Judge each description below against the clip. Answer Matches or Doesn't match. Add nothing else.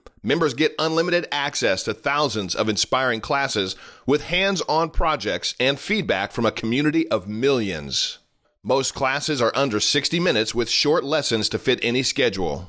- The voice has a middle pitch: Doesn't match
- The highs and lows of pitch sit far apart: Matches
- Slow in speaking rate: Doesn't match